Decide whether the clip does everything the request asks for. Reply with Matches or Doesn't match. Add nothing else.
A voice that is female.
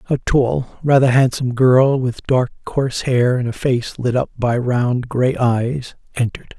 Doesn't match